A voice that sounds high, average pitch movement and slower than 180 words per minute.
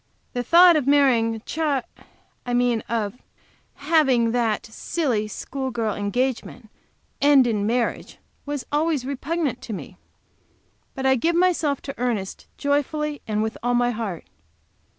Yes: very high, 250 Hz; average, 4.1 semitones; slow, 135 wpm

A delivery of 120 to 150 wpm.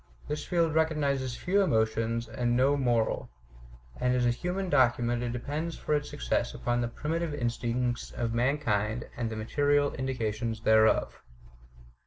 Yes: average, 145 wpm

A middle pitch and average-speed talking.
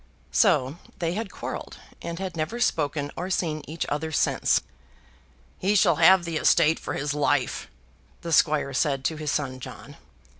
Yes: medium, 160 Hz; average, 160 wpm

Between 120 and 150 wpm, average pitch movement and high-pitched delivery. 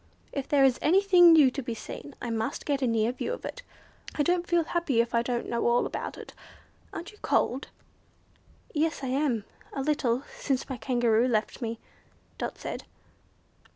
No: average, 185 wpm; average, 4.5 semitones; very high, 265 Hz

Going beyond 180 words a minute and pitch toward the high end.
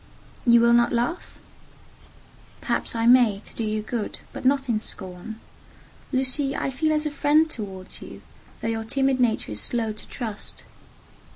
No: average, 165 wpm; high, 235 Hz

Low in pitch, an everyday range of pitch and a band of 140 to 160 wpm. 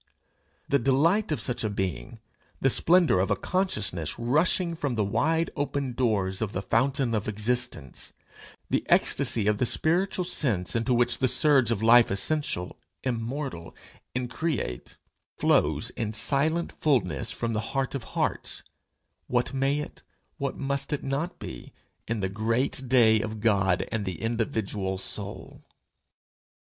Yes: low, 120 Hz; average, 4.8 semitones; average, 145 wpm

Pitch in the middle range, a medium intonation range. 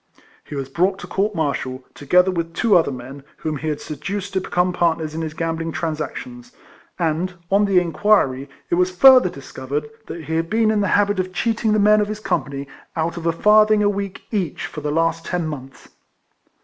Yes: medium, 170 Hz; average, 4.6 semitones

